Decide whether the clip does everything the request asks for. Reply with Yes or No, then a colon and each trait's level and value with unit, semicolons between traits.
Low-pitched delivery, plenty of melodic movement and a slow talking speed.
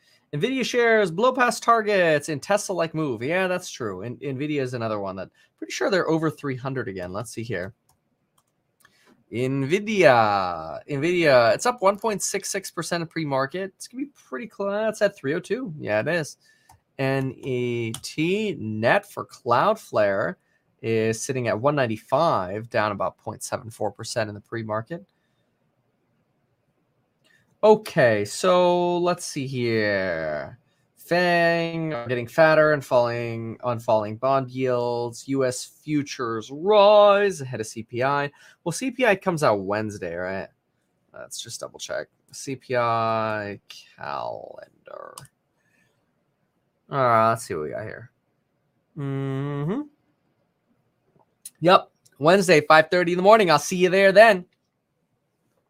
No: medium, 145 Hz; wide, 7.6 semitones; slow, 125 wpm